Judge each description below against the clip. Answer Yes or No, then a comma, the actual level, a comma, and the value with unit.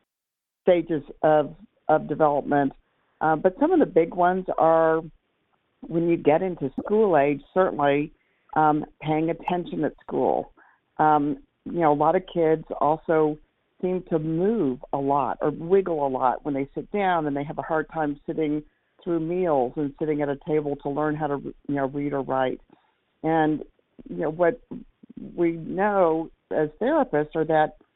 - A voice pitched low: No, medium, 155 Hz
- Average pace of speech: Yes, average, 165 wpm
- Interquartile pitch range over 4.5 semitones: No, narrow, 2.6 semitones